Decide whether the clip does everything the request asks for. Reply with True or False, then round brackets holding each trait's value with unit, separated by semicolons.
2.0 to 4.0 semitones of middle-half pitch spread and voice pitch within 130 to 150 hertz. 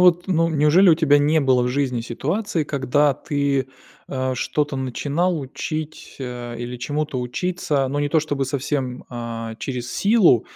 True (3.7 semitones; 140 Hz)